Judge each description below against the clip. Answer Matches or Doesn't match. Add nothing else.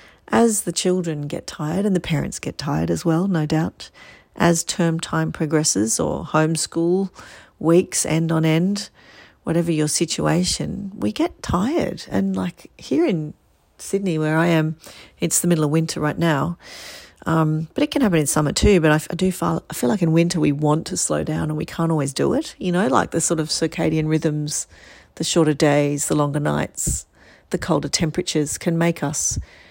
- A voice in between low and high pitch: Matches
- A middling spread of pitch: Doesn't match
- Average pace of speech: Matches